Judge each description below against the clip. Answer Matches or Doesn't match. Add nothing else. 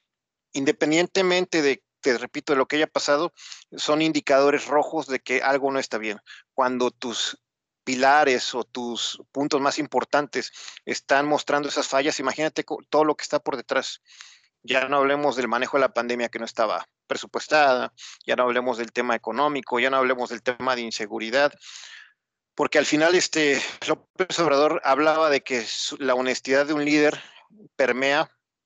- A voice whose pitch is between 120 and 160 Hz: Matches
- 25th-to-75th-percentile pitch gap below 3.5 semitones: Matches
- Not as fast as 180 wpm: Matches